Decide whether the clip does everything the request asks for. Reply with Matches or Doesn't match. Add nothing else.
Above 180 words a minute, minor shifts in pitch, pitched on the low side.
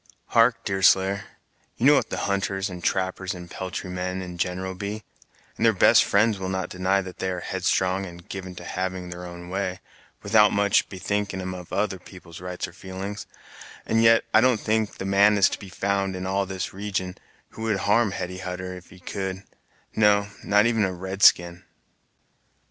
Matches